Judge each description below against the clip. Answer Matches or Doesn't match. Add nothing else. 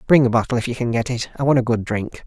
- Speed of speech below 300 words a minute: Doesn't match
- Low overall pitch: Matches